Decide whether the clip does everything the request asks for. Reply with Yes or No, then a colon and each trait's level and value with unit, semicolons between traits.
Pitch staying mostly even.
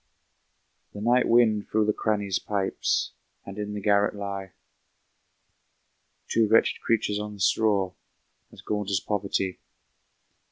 Yes: narrow, 1.4 semitones